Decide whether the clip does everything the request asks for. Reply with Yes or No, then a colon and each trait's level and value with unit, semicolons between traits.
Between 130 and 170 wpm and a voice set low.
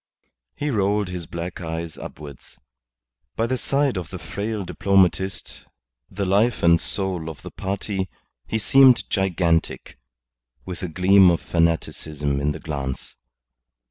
Yes: slow, 135 wpm; very low, 95 Hz